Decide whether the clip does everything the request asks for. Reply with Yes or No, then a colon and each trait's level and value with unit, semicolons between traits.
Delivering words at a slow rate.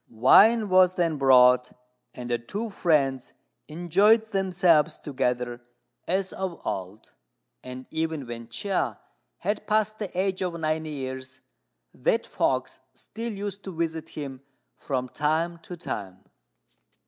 Yes: slow, 125 wpm